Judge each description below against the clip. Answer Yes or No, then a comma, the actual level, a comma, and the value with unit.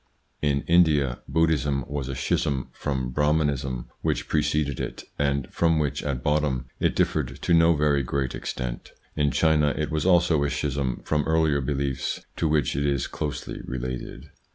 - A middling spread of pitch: No, narrow, 2.3 semitones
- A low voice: Yes, very low, 70 Hz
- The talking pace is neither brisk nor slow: Yes, average, 160 wpm